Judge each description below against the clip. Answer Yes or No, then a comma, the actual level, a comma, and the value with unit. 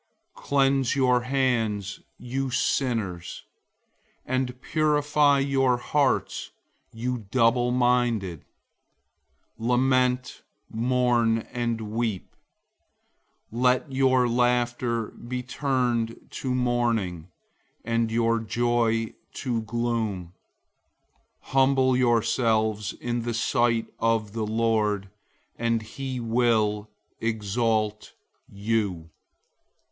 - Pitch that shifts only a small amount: Yes, narrow, 2.1 semitones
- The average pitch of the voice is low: Yes, low, 120 Hz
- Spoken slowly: Yes, slow, 85 wpm